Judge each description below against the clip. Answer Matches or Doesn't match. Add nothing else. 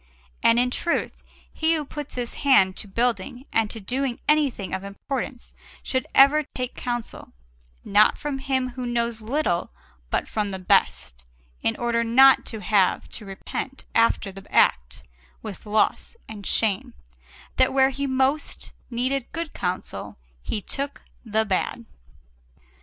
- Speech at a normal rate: Matches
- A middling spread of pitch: Matches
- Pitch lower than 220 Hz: Doesn't match